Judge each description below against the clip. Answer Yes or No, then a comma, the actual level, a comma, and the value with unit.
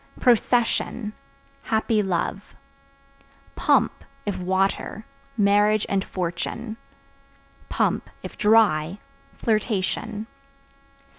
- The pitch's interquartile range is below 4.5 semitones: Yes, narrow, 2.5 semitones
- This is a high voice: Yes, high, 210 Hz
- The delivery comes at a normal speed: No, slow, 65 wpm